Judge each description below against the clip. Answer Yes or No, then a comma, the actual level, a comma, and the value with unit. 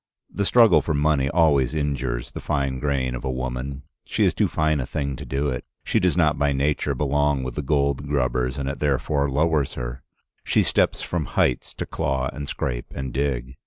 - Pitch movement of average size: No, narrow, 2.2 semitones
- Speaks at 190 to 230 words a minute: Yes, average, 200 wpm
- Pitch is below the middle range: Yes, very low, 70 Hz